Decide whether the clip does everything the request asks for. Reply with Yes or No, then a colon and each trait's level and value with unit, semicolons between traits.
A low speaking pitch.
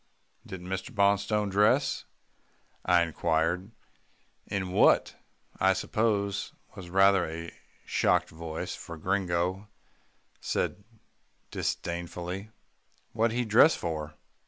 Yes: very low, 95 Hz